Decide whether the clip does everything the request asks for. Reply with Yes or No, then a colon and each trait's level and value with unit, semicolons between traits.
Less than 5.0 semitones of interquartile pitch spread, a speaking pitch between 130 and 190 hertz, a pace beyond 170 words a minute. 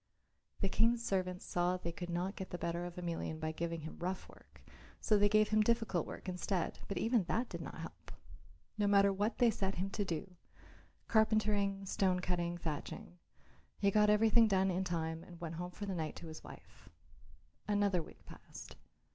Yes: average, 3.1 semitones; medium, 185 Hz; average, 190 wpm